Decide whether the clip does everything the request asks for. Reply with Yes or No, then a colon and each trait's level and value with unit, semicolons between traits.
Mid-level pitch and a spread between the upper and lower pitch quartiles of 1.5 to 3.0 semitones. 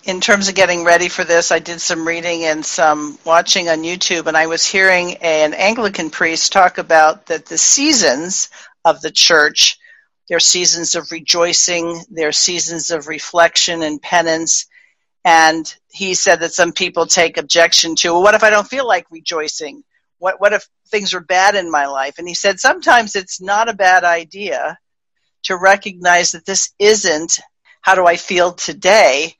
Yes: medium, 175 Hz; narrow, 2.6 semitones